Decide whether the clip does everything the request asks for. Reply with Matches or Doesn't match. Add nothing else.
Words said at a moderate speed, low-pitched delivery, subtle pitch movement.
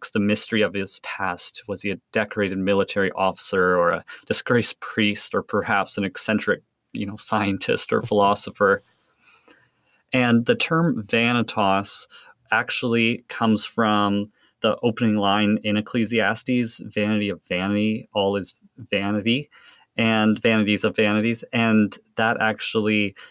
Doesn't match